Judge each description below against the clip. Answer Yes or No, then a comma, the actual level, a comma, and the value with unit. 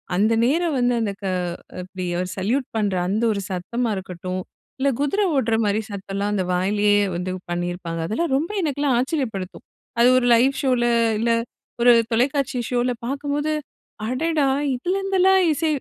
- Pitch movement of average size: No, wide, 6.0 semitones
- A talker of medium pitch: No, high, 240 Hz